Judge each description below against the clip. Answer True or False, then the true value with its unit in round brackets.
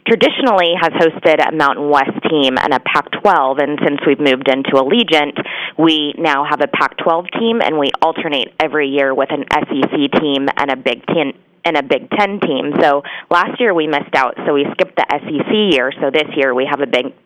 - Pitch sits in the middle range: True (155 Hz)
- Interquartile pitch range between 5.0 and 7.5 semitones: False (4.0 semitones)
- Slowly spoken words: False (205 wpm)